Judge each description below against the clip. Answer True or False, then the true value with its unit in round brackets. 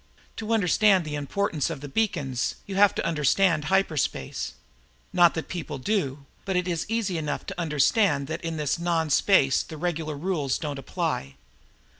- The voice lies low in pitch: False (165 Hz)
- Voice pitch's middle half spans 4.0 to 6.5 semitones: True (4.5 semitones)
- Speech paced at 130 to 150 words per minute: False (170 wpm)